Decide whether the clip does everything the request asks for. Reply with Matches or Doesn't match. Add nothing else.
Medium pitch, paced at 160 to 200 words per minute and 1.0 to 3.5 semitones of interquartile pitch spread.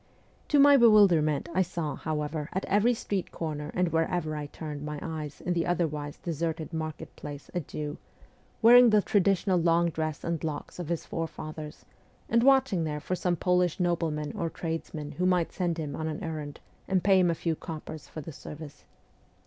Matches